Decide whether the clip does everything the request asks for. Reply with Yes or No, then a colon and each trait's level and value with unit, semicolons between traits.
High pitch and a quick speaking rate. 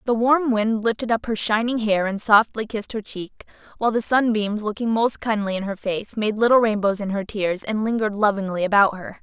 Yes: high, 215 Hz; fast, 215 wpm